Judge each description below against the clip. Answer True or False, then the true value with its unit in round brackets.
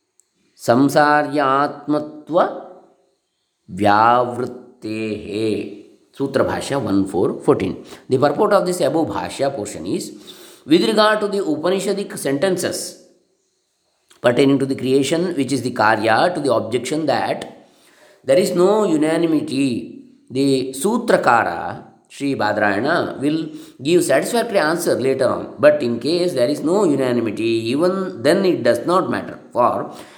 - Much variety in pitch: True (5.9 semitones)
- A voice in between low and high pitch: True (150 Hz)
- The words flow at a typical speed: False (115 wpm)